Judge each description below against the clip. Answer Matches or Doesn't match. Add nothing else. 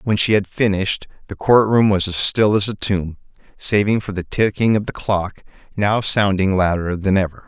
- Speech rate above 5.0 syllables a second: Doesn't match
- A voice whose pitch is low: Matches